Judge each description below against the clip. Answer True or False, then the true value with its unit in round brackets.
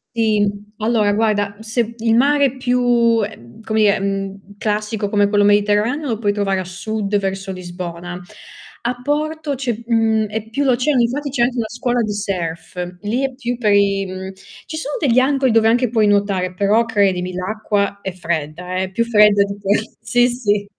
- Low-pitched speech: False (210 Hz)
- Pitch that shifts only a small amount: False (3.2 semitones)